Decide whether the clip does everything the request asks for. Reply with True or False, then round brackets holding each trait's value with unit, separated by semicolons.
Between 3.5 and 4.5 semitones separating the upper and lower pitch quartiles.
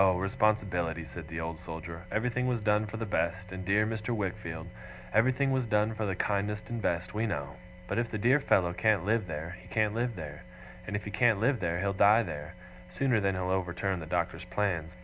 True (3.9 semitones)